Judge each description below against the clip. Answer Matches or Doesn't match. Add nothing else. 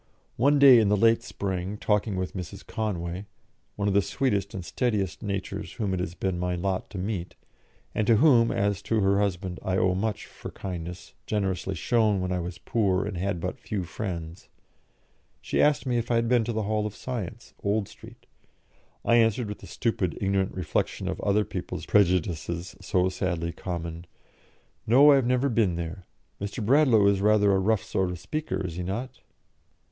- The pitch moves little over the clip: Doesn't match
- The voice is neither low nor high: Doesn't match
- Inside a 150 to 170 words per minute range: Doesn't match